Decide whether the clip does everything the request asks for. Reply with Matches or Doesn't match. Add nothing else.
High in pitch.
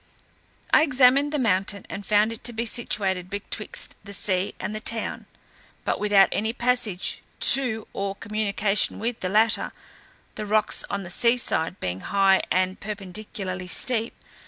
Matches